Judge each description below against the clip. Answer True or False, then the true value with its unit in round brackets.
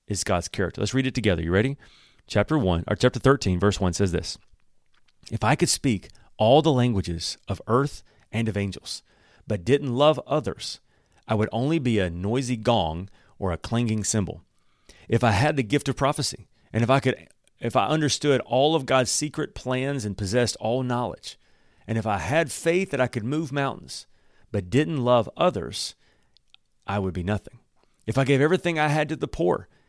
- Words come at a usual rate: True (190 wpm)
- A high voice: False (120 Hz)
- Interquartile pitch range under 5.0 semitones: False (5.3 semitones)